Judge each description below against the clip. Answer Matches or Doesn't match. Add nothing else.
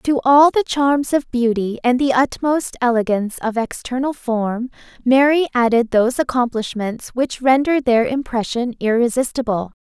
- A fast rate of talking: Doesn't match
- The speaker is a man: Doesn't match